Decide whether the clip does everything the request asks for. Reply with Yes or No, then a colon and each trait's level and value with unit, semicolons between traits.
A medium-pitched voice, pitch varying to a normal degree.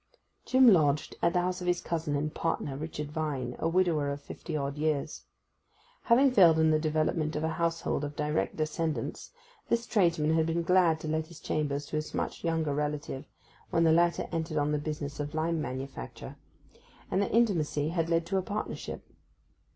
No: medium, 160 Hz; narrow, 2.3 semitones